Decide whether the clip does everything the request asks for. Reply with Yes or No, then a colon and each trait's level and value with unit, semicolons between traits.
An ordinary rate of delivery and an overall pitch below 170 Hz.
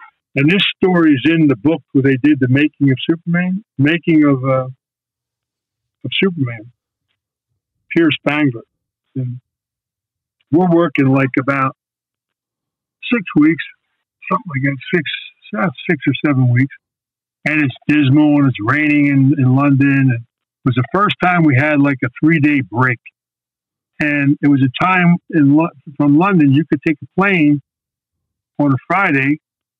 Yes: average, 150 wpm; medium, 140 Hz